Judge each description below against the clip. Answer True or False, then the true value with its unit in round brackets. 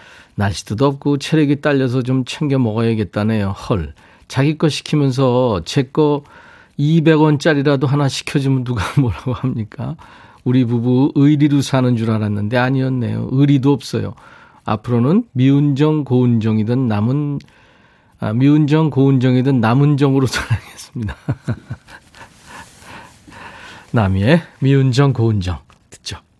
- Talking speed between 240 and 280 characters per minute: True (265 characters per minute)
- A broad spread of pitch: False (3.8 semitones)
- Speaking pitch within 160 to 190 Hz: False (130 Hz)